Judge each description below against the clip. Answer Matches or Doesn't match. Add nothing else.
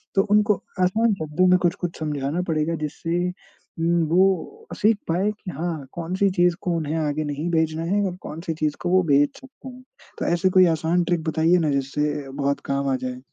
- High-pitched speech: Doesn't match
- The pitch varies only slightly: Doesn't match